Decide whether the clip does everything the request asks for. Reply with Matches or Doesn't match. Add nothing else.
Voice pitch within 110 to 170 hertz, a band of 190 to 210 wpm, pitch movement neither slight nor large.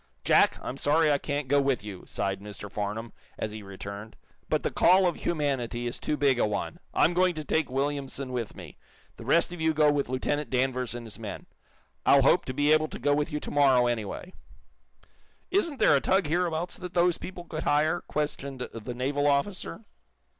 Matches